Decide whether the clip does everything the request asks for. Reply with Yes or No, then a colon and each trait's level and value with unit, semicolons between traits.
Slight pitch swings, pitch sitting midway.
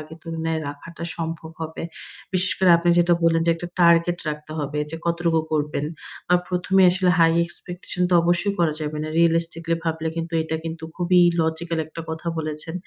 Yes: narrow, 1.3 semitones; medium, 165 Hz